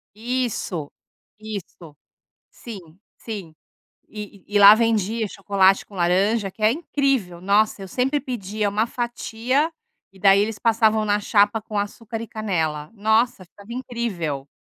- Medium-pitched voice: No, high, 210 Hz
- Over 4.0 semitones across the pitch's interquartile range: No, average, 2.8 semitones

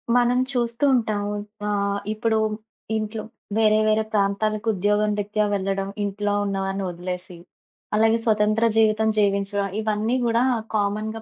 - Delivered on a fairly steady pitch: Yes, narrow, 1.7 semitones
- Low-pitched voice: No, high, 210 Hz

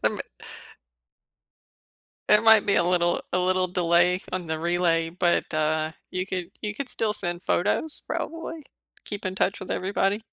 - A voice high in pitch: No, medium, 180 Hz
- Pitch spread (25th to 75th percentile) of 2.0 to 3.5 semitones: Yes, average, 2.8 semitones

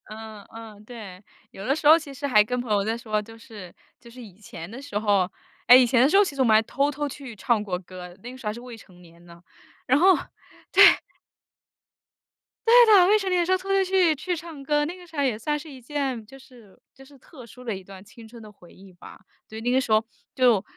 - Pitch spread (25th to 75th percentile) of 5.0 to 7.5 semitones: Yes, average, 5.3 semitones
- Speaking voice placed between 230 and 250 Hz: Yes, high, 240 Hz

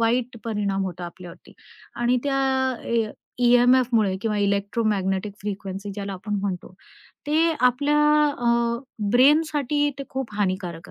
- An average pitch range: Yes, average, 4.2 semitones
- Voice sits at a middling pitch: No, high, 225 Hz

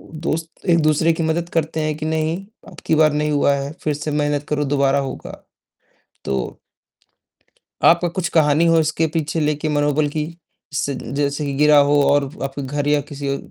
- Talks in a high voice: No, medium, 150 Hz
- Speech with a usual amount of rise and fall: No, narrow, 1.7 semitones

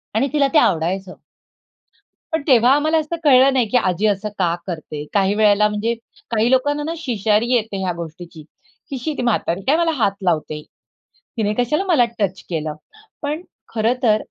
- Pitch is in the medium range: No, high, 220 Hz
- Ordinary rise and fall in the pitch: No, wide, 6.1 semitones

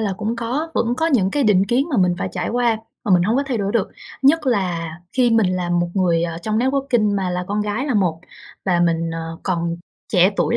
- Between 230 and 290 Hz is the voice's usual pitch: No, high, 205 Hz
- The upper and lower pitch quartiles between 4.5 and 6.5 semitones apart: Yes, wide, 5.5 semitones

